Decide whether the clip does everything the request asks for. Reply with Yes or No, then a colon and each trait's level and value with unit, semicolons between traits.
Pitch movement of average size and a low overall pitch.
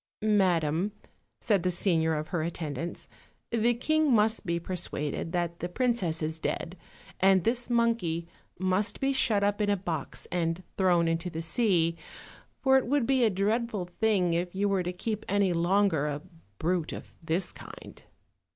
No: average, 4.4 semitones; medium, 185 Hz